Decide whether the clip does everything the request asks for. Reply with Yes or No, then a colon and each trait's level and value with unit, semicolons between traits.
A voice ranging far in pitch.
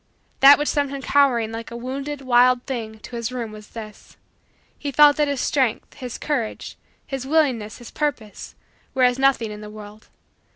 No: average, 3.8 semitones